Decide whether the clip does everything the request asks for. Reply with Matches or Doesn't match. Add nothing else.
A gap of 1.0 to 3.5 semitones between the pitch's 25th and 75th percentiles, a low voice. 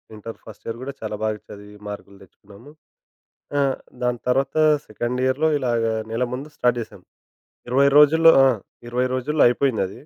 Doesn't match